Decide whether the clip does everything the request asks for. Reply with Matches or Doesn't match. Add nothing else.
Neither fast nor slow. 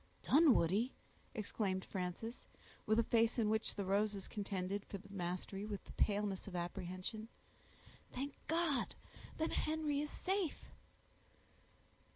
Doesn't match